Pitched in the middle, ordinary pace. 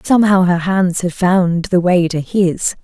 Yes: medium, 180 Hz; average, 190 wpm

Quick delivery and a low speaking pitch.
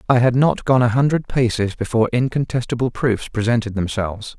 No: average, 165 wpm; low, 120 Hz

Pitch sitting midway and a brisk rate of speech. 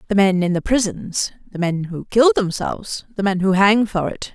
No: high, 195 Hz; fast, 220 wpm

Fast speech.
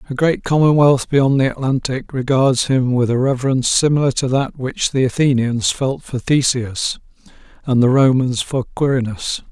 No: average, 160 wpm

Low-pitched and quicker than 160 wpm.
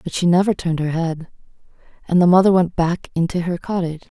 No: medium, 175 Hz; average, 200 wpm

